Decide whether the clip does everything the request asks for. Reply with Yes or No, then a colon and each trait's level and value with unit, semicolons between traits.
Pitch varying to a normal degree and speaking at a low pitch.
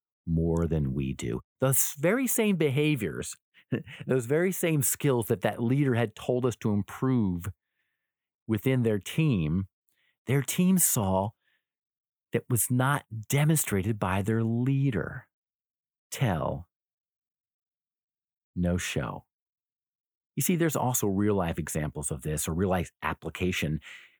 No: wide, 6.9 semitones; low, 115 Hz